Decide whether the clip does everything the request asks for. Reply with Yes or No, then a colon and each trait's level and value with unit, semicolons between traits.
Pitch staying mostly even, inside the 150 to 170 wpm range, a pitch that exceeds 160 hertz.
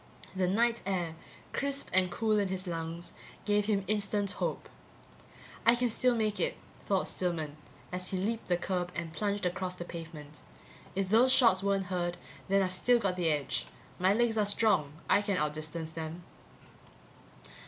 No: average, 3.2 semitones; average, 165 wpm; high, 190 Hz